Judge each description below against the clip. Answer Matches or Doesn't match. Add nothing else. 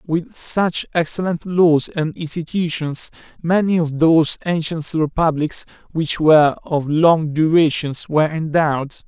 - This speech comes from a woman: Doesn't match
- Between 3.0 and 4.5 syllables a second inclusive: Matches